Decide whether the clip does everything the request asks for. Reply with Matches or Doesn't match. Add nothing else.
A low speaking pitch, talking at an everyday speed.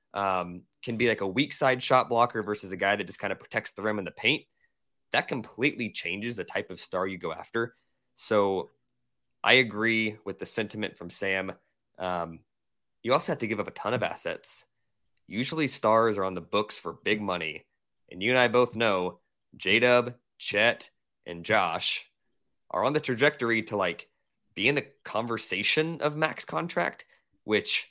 Matches